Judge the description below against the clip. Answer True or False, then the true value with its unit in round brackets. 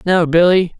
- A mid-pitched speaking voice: True (175 Hz)